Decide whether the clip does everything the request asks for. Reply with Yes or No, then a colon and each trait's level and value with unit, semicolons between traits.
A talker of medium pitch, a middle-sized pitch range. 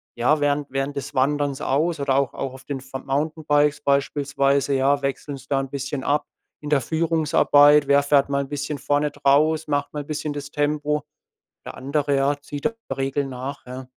No: medium, 145 Hz; narrow, 1.2 semitones